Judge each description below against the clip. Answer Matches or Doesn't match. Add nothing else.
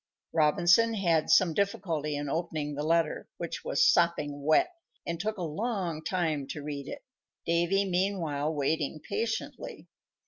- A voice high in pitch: Doesn't match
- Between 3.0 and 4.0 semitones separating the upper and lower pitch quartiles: Doesn't match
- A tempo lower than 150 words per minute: Matches